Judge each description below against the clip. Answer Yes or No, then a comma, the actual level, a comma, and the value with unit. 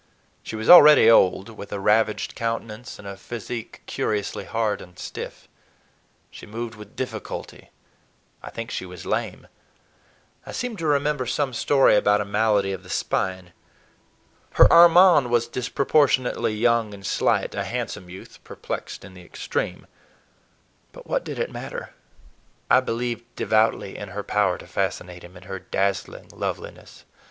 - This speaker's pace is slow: No, average, 145 wpm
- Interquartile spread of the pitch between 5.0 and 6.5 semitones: No, average, 3.7 semitones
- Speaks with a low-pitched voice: Yes, low, 110 Hz